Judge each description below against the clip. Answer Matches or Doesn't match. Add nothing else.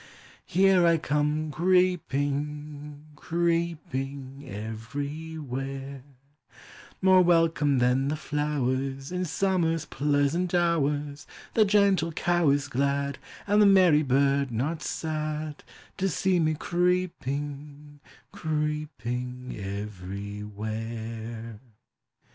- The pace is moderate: Doesn't match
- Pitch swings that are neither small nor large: Matches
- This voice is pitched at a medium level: Matches